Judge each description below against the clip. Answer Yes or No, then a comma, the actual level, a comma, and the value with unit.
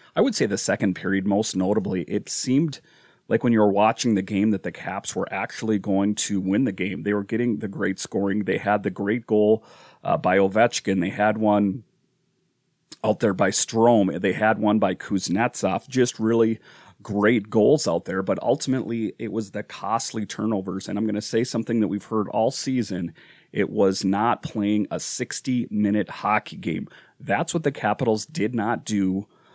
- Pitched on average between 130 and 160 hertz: No, low, 105 Hz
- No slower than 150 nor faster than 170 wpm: No, average, 190 wpm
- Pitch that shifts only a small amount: Yes, narrow, 2.0 semitones